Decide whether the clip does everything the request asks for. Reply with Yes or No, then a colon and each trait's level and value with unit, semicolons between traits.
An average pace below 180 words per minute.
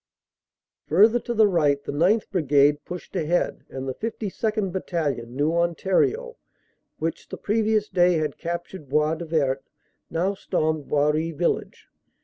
Yes: slow, 135 wpm